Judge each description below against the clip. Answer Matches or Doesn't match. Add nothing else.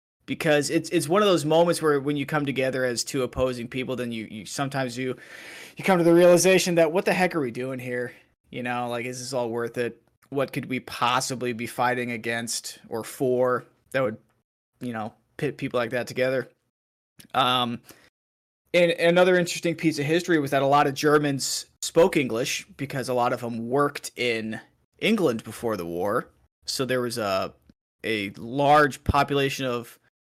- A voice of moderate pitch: Doesn't match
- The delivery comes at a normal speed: Matches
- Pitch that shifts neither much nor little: Matches